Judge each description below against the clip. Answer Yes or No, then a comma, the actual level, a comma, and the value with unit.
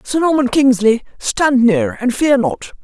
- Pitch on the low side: No, very high, 260 Hz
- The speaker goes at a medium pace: Yes, average, 170 wpm